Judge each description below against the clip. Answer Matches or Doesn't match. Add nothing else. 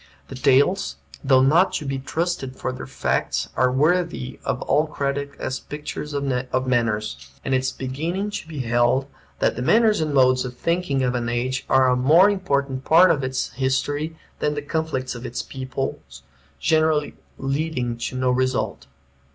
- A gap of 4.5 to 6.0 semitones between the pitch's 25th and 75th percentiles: Doesn't match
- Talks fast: Doesn't match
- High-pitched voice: Doesn't match